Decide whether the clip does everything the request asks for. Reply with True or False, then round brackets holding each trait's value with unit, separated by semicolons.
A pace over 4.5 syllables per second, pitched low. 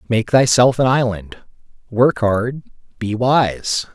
False (3.4 syllables/s; 120 Hz)